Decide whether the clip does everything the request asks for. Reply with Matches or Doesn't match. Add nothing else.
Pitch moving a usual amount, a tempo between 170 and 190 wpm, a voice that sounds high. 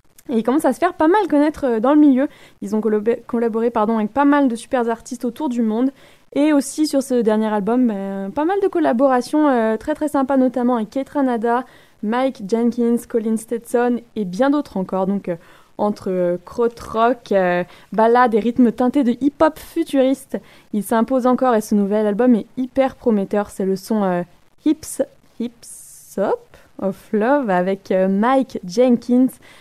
Matches